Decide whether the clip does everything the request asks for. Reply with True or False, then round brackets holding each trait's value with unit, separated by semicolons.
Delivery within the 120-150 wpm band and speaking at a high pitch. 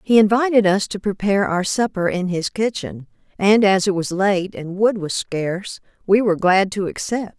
False (195 wpm; 195 Hz)